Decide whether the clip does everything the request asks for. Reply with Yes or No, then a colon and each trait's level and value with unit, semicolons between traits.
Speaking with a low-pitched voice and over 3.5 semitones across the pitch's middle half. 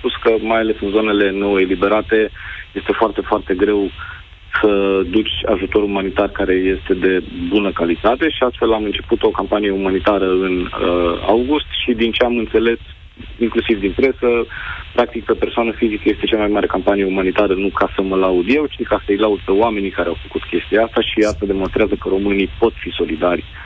No: low, 100 Hz; average, 2.7 semitones